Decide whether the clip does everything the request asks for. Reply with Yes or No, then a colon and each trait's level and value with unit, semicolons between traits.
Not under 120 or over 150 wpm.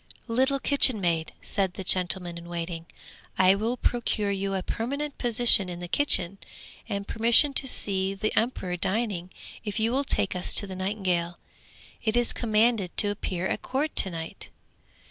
No: average, 165 wpm